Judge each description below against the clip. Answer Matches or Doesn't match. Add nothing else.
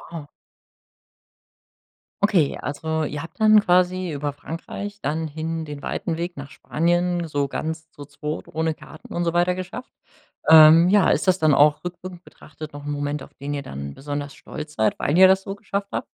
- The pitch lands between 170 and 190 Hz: Doesn't match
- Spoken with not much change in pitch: Doesn't match